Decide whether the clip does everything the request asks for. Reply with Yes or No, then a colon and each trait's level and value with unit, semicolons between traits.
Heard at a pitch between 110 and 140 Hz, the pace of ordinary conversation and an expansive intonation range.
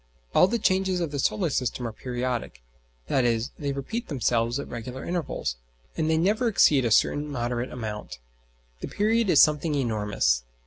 Yes: low, 135 Hz; average, 165 wpm; wide, 6.4 semitones